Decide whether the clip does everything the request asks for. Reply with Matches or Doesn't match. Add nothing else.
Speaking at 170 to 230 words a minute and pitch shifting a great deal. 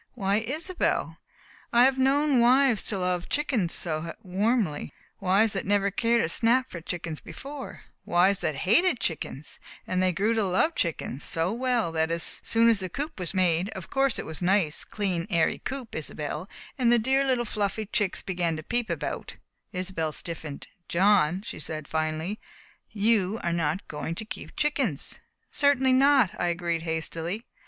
Matches